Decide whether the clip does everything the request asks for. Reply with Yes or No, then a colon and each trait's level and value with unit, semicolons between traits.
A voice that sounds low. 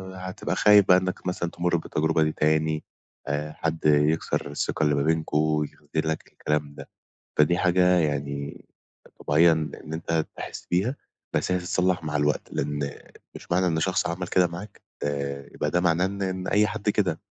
Yes: very low, 80 Hz